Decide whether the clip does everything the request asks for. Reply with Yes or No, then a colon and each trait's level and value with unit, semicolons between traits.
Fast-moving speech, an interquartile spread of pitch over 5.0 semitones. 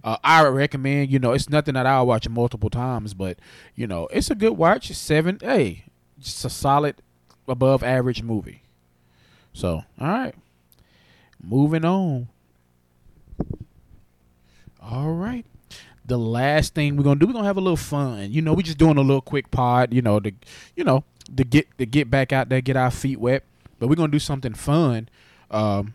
No: average, 185 wpm; wide, 5.6 semitones